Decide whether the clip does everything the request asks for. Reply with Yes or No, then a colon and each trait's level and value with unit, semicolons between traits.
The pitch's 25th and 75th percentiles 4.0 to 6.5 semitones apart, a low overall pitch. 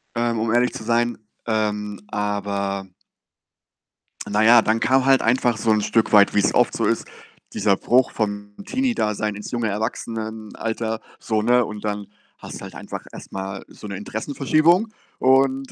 No: average, 2.7 semitones; low, 110 Hz